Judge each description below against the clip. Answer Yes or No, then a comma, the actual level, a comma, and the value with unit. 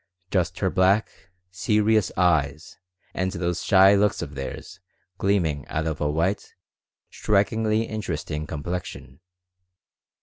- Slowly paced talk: Yes, slow, 110 wpm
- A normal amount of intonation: Yes, average, 4.3 semitones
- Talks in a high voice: No, very low, 95 Hz